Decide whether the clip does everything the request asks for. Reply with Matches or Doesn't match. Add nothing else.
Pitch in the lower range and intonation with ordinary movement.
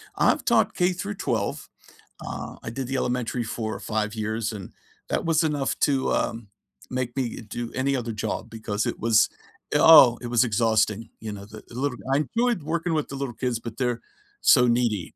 Matches